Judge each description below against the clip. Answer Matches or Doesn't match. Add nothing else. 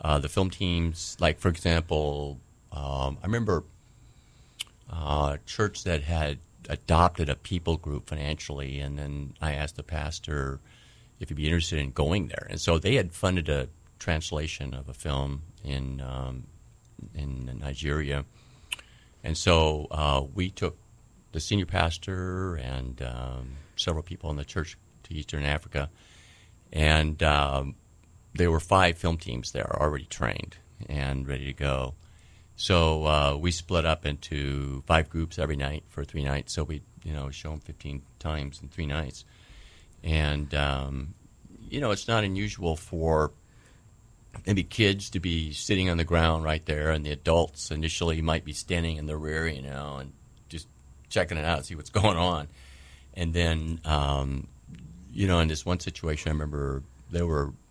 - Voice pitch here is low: Matches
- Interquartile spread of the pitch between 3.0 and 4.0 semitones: Matches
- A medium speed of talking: Matches